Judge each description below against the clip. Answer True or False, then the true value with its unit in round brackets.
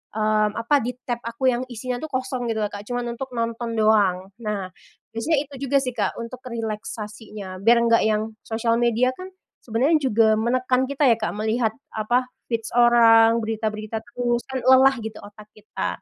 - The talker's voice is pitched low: False (230 Hz)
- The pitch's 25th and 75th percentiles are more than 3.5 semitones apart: False (2.5 semitones)